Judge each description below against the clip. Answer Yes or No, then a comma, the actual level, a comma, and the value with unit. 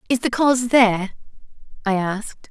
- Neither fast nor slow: Yes, average, 145 wpm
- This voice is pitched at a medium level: No, high, 220 Hz